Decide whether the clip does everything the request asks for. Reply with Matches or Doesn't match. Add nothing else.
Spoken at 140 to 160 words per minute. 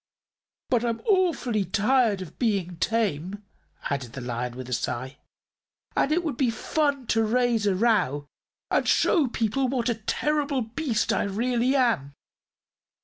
Matches